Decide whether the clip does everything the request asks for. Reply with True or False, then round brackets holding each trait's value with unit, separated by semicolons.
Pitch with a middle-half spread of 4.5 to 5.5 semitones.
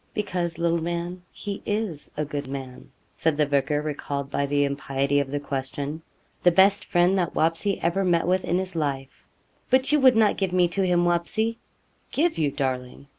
True (4.9 semitones)